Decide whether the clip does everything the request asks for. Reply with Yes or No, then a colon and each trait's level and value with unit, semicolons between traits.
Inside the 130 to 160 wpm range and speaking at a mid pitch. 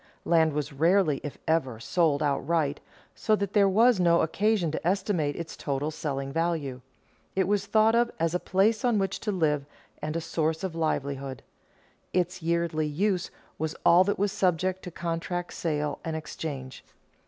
No: average, 170 wpm; medium, 165 Hz